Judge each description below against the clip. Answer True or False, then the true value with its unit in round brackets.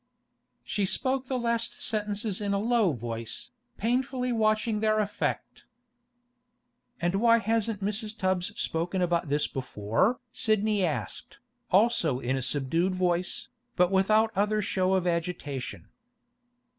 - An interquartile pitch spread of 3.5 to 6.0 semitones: True (4.2 semitones)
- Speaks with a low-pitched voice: False (200 Hz)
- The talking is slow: True (125 wpm)